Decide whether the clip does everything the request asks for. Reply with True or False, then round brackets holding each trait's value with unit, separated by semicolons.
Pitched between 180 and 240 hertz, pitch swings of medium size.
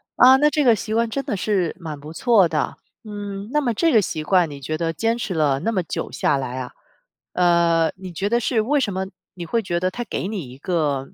False (185 Hz; 5.8 semitones)